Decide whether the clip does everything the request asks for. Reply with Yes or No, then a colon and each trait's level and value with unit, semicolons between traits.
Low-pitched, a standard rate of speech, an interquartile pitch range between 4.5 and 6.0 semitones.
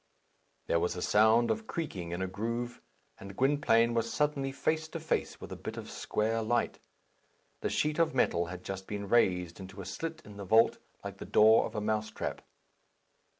Yes: low, 110 Hz; average, 195 wpm; average, 5.1 semitones